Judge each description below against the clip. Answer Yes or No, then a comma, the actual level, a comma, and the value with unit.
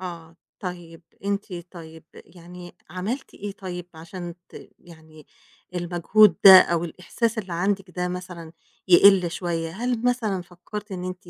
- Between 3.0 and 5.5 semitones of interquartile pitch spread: No, narrow, 2.4 semitones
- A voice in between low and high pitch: Yes, medium, 180 Hz